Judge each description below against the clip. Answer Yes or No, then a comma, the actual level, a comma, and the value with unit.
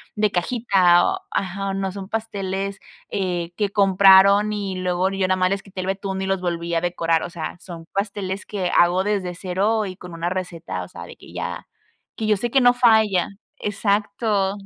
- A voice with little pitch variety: Yes, narrow, 2.2 semitones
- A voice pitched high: Yes, high, 195 Hz